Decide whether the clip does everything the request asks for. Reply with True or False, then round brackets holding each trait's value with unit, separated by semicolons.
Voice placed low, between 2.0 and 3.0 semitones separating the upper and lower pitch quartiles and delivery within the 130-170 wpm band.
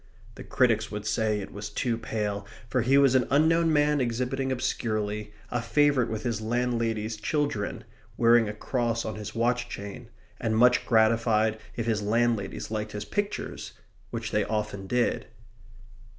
True (115 Hz; 2.6 semitones; 155 wpm)